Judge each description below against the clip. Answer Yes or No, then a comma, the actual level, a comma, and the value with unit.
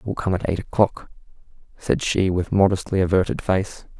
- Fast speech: No, average, 180 wpm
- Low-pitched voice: Yes, very low, 95 Hz